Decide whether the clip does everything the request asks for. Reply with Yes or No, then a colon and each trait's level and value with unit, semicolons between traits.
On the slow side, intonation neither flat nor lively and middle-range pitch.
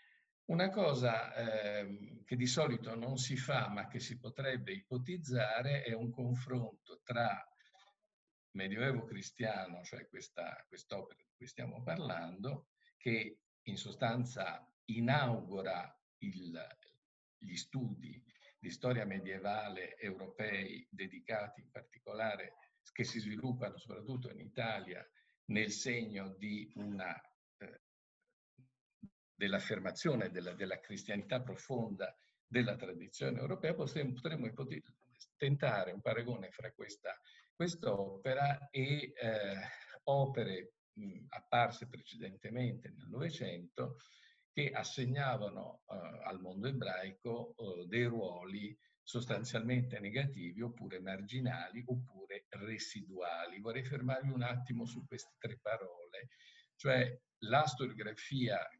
No: slow, 105 wpm; average, 4.0 semitones; low, 125 Hz